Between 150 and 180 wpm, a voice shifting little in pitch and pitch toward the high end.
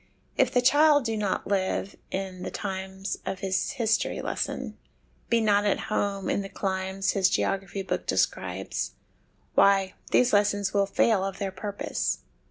Yes: average, 155 wpm; narrow, 1.6 semitones; high, 195 Hz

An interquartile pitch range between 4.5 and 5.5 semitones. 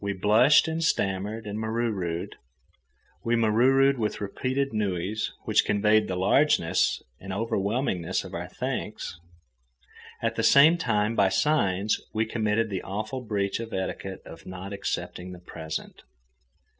No: average, 3.4 semitones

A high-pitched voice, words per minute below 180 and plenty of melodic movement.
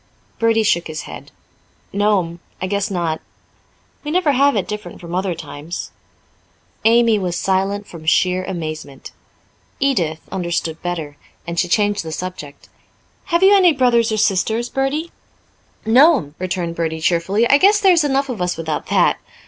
Yes: high, 195 Hz; average, 150 wpm; wide, 6.1 semitones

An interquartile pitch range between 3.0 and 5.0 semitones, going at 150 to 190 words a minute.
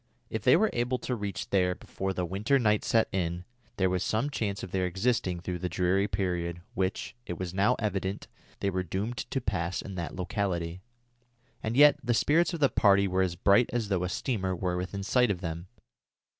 No: average, 3.5 semitones; fast, 205 wpm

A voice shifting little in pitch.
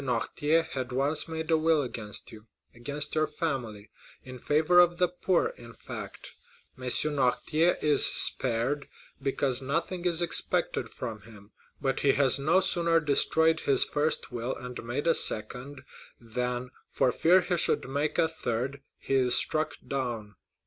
No: average, 4.5 semitones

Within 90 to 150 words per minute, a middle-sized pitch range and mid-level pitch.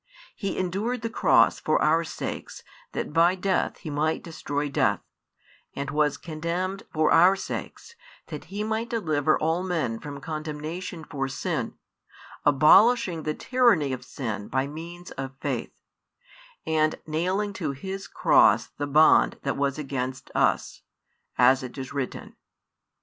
Yes: average, 140 wpm; average, 4.6 semitones; medium, 155 Hz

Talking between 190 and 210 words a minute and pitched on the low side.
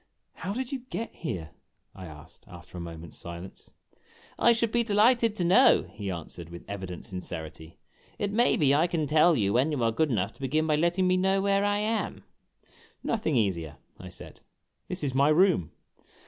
No: average, 195 wpm; medium, 150 Hz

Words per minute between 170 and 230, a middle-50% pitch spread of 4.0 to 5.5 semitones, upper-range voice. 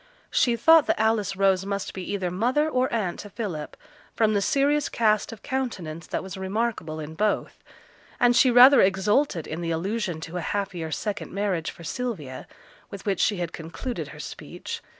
Yes: average, 180 wpm; average, 5.1 semitones; high, 200 Hz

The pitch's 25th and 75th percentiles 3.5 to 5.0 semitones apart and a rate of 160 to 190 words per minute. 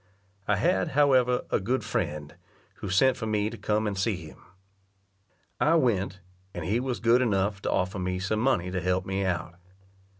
Yes: average, 4.6 semitones; average, 180 wpm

